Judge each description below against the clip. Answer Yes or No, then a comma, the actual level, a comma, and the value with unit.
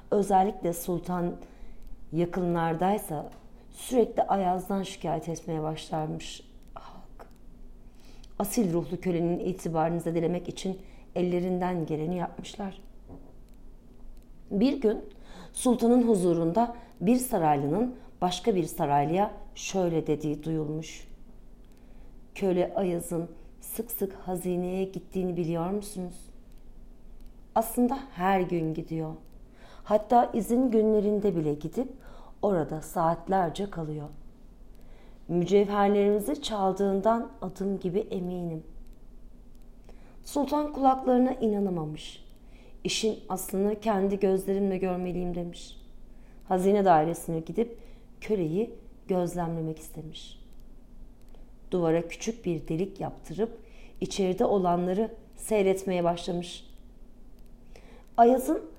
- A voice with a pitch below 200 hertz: Yes, medium, 185 Hz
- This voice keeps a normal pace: No, slow, 80 wpm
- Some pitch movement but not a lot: Yes, average, 3.9 semitones